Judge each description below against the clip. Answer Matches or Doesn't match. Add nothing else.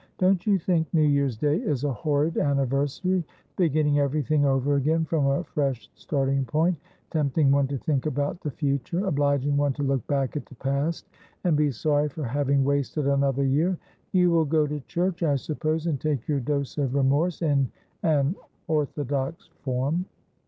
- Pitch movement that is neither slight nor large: Doesn't match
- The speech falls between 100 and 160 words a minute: Doesn't match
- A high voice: Doesn't match